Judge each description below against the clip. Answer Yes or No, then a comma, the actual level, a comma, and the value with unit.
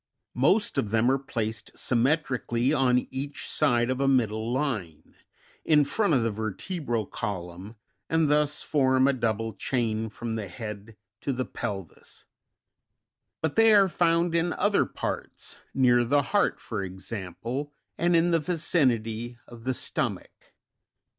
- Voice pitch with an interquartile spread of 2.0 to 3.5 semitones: No, average, 5.1 semitones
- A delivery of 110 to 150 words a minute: Yes, average, 140 wpm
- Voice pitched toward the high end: No, low, 125 Hz